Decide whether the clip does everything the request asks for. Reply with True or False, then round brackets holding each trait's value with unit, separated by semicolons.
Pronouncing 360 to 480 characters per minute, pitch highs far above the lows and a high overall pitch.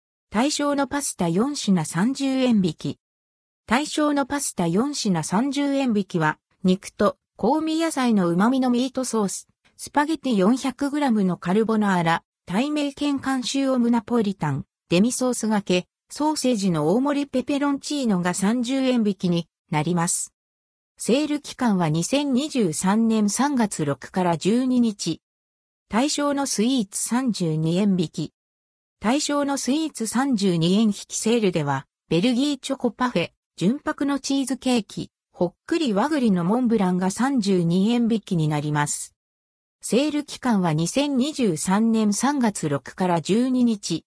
False (245 characters per minute; 7.1 semitones; 220 Hz)